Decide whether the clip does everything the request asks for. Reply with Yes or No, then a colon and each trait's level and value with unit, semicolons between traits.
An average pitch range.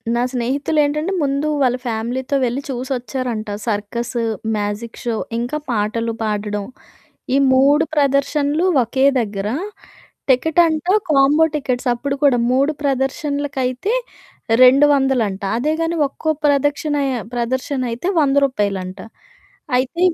Yes: average, 3.4 semitones